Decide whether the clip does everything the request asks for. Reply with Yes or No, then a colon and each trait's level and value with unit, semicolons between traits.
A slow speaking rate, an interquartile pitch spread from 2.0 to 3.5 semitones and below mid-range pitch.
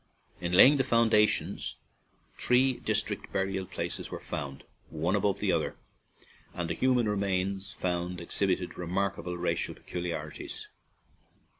Yes: slow, 125 wpm; average, 3.1 semitones; very low, 95 Hz